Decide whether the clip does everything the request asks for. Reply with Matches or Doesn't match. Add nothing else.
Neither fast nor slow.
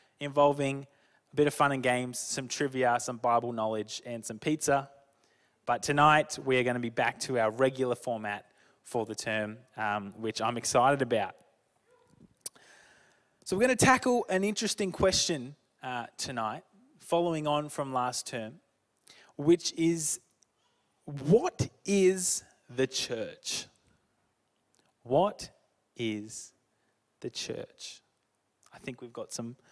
Doesn't match